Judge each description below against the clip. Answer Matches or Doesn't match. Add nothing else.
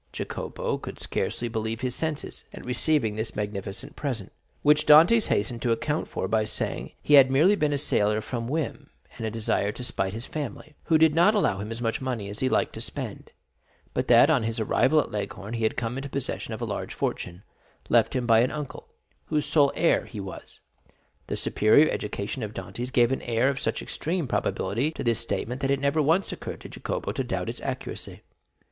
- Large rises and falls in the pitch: Doesn't match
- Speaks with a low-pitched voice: Matches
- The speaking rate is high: Matches